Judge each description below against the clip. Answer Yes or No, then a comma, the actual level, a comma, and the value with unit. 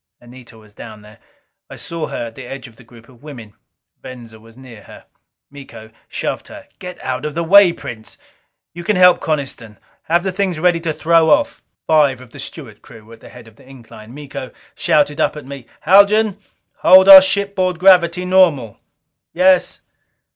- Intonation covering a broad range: Yes, wide, 7.3 semitones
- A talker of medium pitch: Yes, medium, 145 Hz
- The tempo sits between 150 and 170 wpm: No, average, 185 wpm